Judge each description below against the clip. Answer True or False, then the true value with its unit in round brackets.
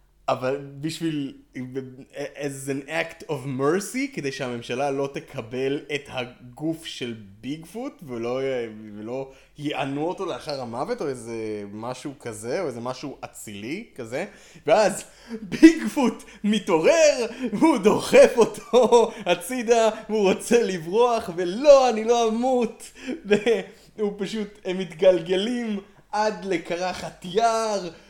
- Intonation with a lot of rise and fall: True (8.6 semitones)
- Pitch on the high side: False (175 Hz)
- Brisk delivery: False (115 wpm)